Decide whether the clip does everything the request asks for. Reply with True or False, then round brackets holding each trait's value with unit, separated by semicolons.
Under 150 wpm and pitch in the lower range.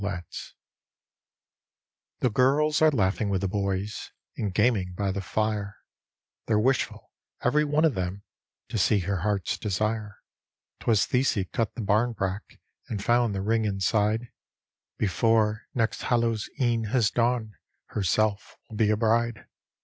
True (140 wpm; 110 Hz)